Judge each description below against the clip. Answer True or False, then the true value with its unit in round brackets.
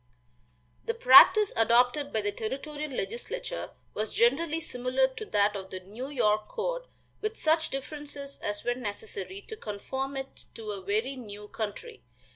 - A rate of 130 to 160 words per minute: True (150 wpm)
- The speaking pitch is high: True (265 Hz)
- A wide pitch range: True (6.8 semitones)